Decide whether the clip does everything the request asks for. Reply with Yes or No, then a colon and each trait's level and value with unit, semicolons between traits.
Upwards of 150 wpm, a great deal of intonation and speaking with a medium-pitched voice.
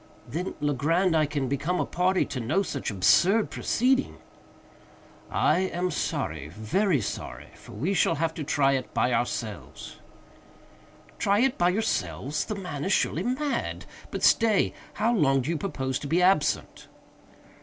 No: average, 140 wpm; wide, 6.1 semitones; medium, 165 Hz